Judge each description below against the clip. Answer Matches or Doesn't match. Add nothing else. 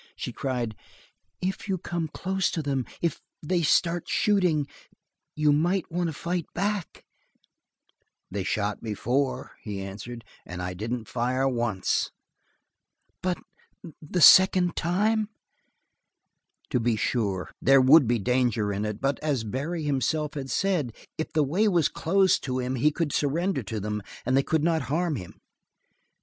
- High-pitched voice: Doesn't match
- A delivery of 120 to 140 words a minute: Doesn't match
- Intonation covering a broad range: Matches